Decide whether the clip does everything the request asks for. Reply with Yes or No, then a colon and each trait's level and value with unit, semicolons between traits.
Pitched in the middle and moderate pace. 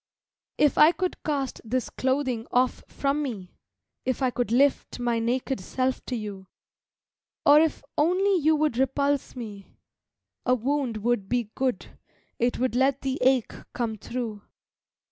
No: very high, 255 Hz; average, 145 wpm